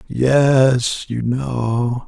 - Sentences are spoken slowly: Yes, slow, 85 wpm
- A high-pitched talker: No, low, 120 Hz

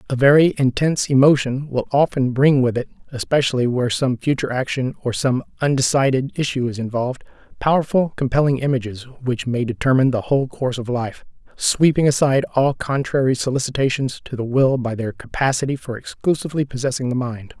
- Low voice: Yes, low, 130 Hz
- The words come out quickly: No, average, 155 wpm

